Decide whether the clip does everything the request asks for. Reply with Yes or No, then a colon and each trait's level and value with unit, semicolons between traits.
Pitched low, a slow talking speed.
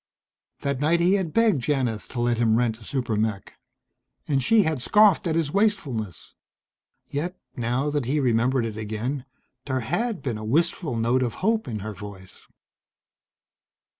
No: low, 130 Hz; average, 165 wpm